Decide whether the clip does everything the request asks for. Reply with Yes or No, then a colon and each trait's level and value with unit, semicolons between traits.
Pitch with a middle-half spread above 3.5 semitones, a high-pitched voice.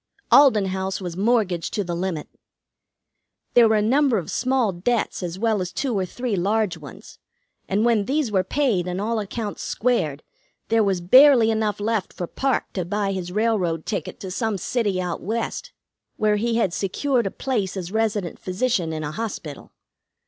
Yes: average, 4.0 semitones; high, 205 Hz